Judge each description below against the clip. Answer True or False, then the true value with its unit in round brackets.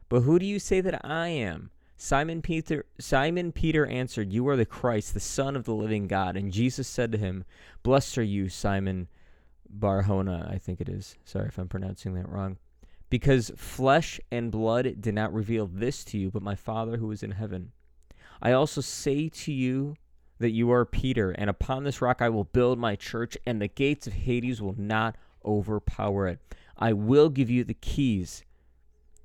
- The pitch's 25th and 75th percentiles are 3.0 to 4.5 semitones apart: False (5.2 semitones)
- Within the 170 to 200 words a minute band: True (190 wpm)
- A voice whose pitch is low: True (110 Hz)